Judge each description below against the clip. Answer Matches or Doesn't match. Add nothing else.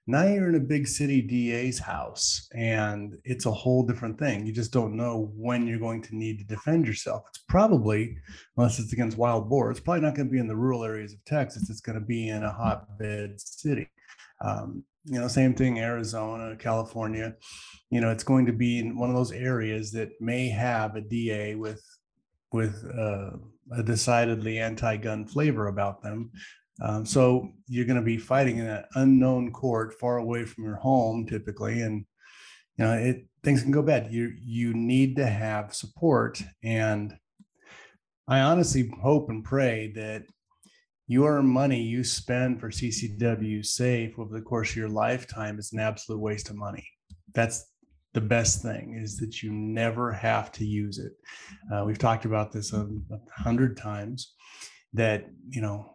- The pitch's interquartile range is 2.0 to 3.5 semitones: Matches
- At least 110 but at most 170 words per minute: Doesn't match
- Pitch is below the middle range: Matches